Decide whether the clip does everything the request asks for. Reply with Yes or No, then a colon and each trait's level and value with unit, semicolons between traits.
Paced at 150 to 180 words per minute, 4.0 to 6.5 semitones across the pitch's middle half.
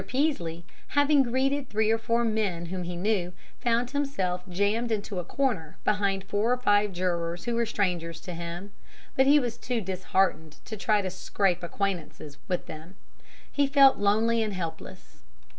Yes: average, 165 wpm; average, 4.9 semitones